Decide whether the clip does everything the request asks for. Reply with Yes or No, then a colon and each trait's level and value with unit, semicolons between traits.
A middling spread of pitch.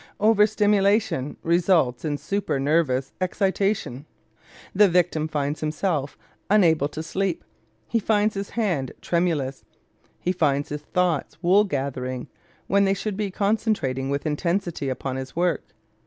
No: wide, 5.8 semitones